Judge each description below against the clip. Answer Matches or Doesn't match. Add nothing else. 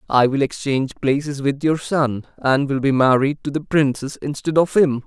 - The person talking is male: Matches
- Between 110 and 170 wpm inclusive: Doesn't match